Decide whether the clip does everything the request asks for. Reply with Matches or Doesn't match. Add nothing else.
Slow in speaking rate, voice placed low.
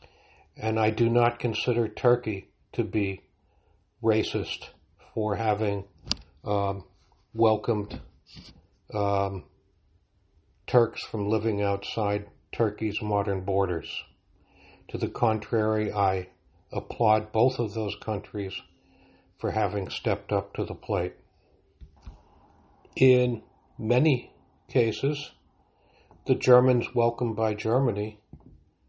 Matches